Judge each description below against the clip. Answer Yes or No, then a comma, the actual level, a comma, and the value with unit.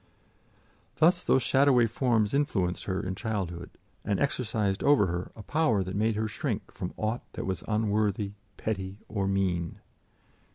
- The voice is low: Yes, low, 105 Hz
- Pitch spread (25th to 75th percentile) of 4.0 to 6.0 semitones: No, average, 3.6 semitones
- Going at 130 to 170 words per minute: Yes, average, 150 wpm